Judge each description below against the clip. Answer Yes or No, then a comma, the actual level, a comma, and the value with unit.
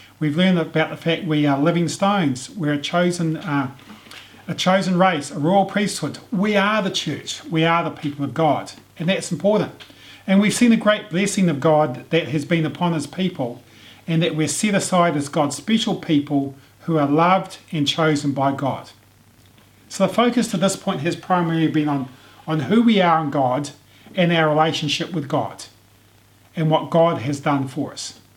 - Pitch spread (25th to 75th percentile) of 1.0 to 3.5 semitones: No, average, 4.4 semitones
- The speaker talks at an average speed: Yes, average, 190 wpm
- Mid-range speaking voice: Yes, medium, 155 Hz